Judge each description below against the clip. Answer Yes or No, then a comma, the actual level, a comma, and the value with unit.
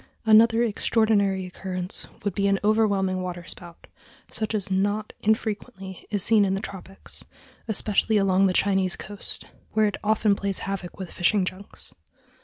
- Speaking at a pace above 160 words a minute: No, average, 145 wpm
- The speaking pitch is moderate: No, high, 200 Hz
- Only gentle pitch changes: Yes, narrow, 2.2 semitones